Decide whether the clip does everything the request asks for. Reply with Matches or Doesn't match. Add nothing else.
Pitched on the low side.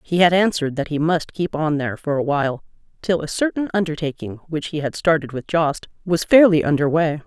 Doesn't match